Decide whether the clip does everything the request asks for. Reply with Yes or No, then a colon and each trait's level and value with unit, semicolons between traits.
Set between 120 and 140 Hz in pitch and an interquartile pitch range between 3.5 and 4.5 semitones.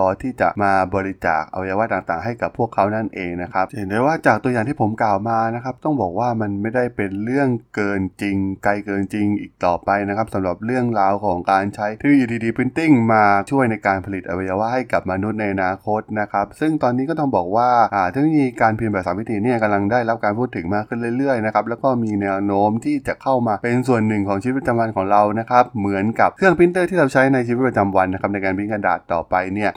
No: low, 105 Hz; average, 3.8 semitones